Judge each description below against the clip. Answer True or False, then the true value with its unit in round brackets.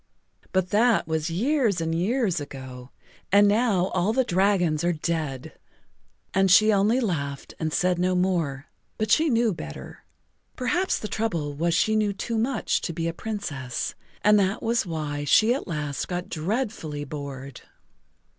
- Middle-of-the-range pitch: True (180 Hz)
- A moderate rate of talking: True (155 wpm)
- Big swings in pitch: True (5.9 semitones)